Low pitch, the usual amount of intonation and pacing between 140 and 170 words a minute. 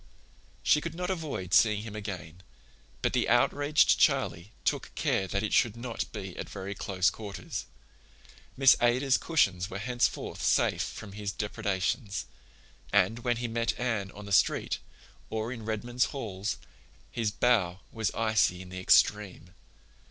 Yes: low, 105 Hz; average, 3.8 semitones; average, 150 wpm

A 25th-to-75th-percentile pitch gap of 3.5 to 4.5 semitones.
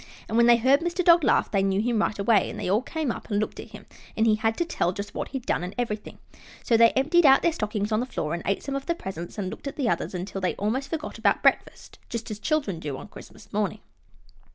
No: average, 5.2 semitones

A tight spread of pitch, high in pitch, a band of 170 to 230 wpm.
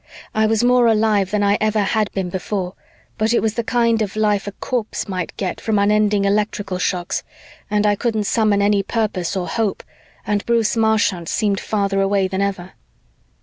Yes: narrow, 1.9 semitones; high, 205 Hz; average, 185 wpm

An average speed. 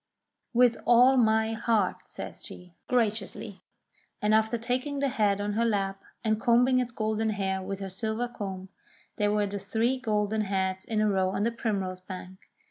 Yes: average, 175 wpm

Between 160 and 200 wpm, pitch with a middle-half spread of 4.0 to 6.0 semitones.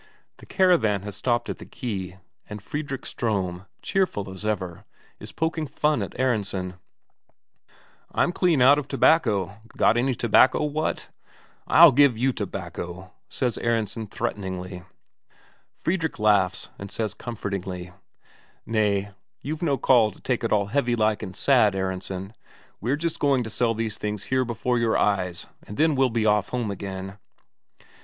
No: average, 150 wpm; average, 5.0 semitones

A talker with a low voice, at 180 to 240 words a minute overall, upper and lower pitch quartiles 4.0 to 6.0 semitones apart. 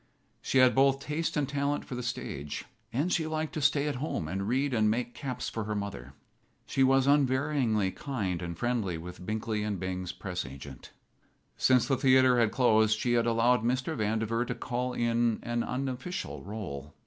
Yes: low, 120 Hz; average, 185 wpm; average, 4.3 semitones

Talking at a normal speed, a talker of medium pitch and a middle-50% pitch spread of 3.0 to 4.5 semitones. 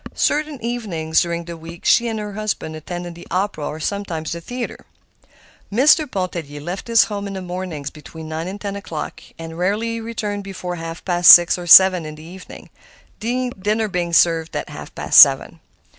Yes: average, 175 wpm; medium, 180 Hz; average, 4.1 semitones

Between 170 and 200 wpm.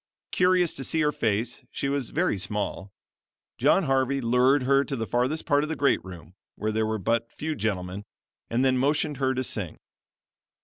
Yes: average, 185 wpm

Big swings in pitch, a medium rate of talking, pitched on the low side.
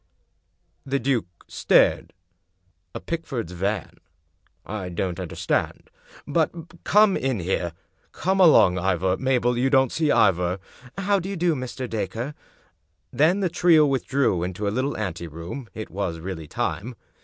Yes: wide, 7.8 semitones; average, 145 wpm; low, 115 Hz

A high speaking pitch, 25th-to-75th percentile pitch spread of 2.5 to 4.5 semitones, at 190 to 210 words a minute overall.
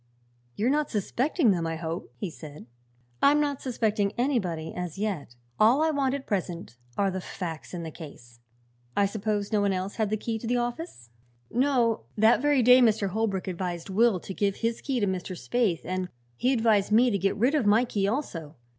No: high, 210 Hz; average, 4.9 semitones; average, 200 wpm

